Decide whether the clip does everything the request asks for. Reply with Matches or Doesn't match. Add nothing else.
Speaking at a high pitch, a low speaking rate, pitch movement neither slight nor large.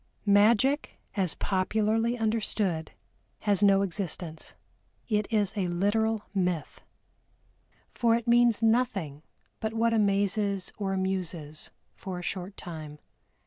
Matches